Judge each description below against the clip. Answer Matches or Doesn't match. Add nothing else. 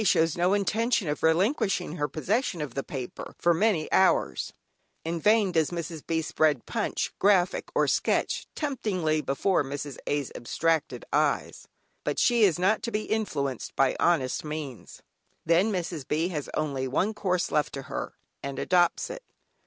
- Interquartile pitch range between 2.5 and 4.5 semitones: Doesn't match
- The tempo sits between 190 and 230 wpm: Doesn't match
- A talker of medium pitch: Matches